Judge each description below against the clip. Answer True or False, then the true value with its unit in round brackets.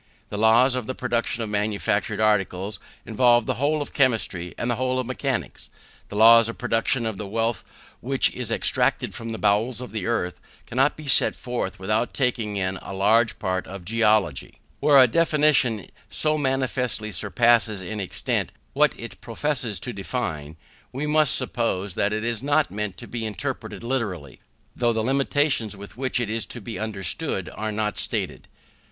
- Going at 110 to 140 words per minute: False (175 wpm)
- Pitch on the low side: True (115 Hz)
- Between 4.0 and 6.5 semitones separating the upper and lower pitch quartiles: False (3.6 semitones)